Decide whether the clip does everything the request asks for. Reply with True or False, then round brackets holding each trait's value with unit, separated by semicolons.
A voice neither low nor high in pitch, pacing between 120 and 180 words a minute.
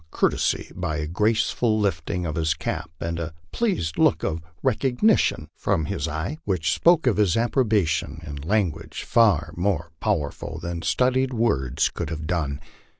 False (85 Hz; 150 wpm)